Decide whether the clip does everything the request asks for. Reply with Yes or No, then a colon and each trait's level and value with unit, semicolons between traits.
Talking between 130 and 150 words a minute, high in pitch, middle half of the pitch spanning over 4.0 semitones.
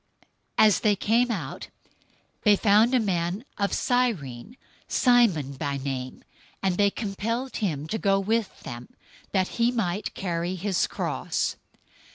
Yes: average, 140 wpm; high, 200 Hz; average, 5.2 semitones